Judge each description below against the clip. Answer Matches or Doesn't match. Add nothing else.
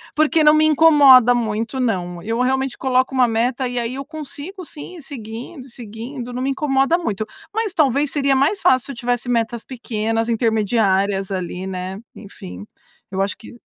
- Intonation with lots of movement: Doesn't match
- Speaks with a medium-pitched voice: Doesn't match